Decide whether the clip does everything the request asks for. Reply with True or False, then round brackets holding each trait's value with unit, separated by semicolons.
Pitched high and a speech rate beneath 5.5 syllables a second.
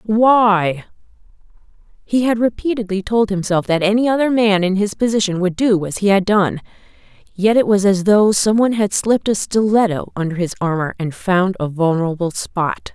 True (200 Hz; 5.1 syllables/s)